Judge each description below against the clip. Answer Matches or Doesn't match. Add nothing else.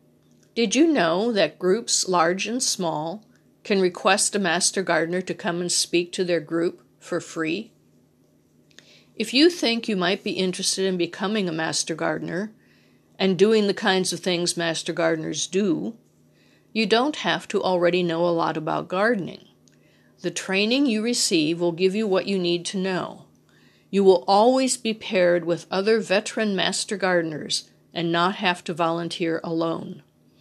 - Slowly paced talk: Doesn't match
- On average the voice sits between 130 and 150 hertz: Doesn't match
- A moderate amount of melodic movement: Matches